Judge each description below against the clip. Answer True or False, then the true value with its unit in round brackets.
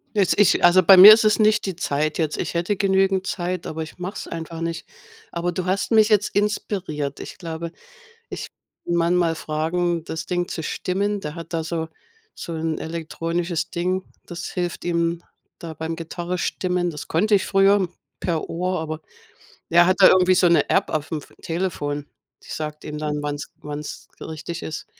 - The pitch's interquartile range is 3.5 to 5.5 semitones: False (2.5 semitones)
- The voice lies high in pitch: False (170 Hz)